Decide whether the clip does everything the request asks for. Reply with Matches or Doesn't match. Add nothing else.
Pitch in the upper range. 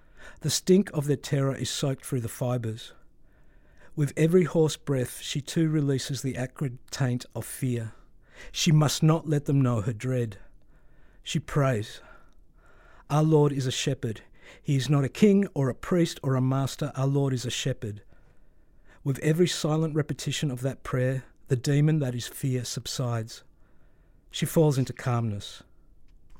Doesn't match